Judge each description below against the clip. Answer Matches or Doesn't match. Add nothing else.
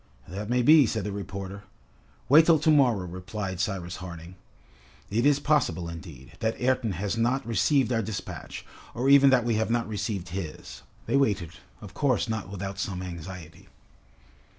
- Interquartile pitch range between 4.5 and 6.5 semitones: Matches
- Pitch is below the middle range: Matches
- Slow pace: Doesn't match